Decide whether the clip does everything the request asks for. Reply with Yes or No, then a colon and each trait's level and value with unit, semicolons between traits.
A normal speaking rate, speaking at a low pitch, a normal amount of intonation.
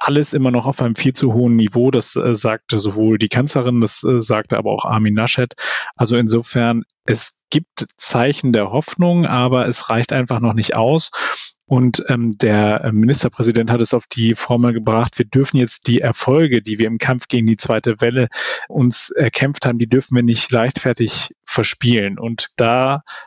No: average, 180 wpm; low, 120 Hz; narrow, 2.2 semitones